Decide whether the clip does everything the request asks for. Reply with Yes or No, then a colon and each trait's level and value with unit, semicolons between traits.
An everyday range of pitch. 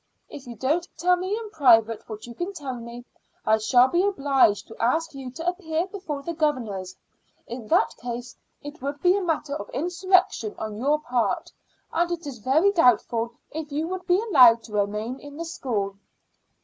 No: wide, 6.6 semitones